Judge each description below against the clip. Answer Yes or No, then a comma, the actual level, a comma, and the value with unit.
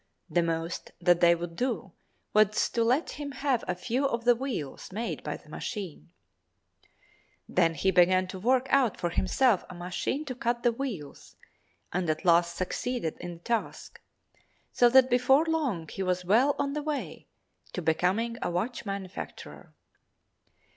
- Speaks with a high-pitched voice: Yes, high, 210 Hz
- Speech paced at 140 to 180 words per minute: Yes, average, 160 wpm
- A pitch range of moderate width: No, wide, 6.2 semitones